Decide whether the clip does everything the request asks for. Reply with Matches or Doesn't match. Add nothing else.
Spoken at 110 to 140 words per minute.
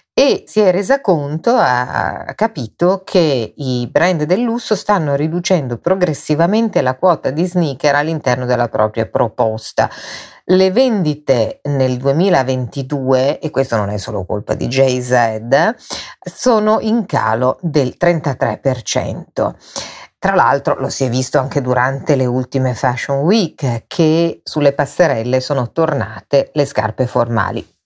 Matches